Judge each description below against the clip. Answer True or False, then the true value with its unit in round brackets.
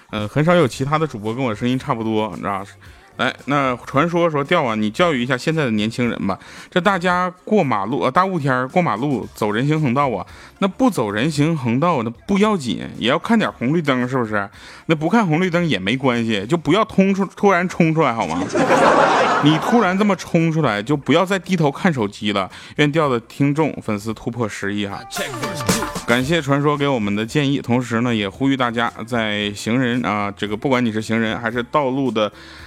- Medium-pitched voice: False (130 Hz)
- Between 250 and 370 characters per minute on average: True (305 characters per minute)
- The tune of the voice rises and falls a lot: True (7.0 semitones)